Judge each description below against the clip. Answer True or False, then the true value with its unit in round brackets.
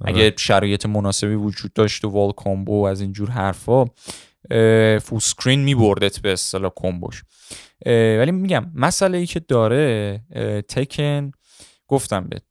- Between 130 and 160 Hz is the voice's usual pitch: False (110 Hz)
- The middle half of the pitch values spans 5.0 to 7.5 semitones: False (4.3 semitones)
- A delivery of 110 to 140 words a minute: True (130 wpm)